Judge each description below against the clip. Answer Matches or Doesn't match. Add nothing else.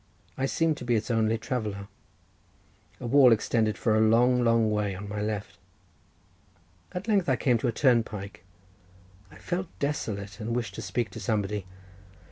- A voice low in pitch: Matches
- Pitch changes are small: Doesn't match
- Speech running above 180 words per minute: Doesn't match